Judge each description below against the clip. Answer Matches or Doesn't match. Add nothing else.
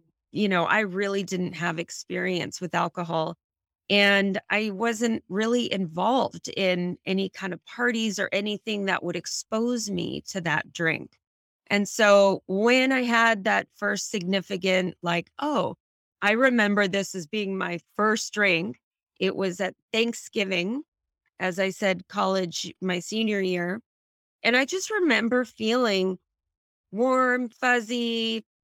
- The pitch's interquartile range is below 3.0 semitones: Doesn't match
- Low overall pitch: Doesn't match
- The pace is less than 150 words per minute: Matches